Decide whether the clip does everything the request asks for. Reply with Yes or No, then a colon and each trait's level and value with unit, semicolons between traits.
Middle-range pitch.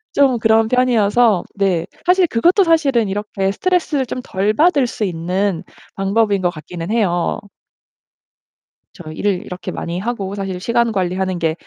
No: high, 205 Hz